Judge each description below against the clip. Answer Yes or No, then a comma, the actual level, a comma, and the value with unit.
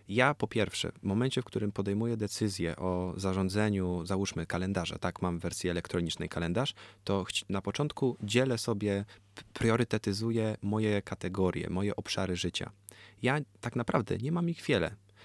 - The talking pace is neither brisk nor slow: Yes, average, 150 wpm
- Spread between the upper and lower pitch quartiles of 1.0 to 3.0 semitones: No, average, 3.6 semitones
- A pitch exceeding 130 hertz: No, low, 100 Hz